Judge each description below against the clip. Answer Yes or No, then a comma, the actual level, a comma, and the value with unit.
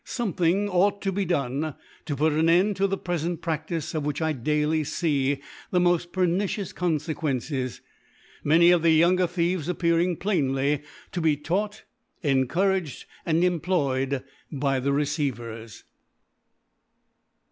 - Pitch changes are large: No, average, 3.8 semitones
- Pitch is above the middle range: No, medium, 160 Hz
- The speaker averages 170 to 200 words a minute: No, slow, 135 wpm